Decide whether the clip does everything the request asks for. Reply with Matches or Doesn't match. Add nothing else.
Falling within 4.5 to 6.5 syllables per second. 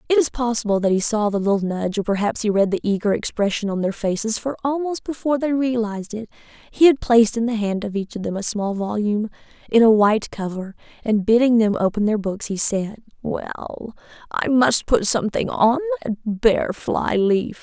Matches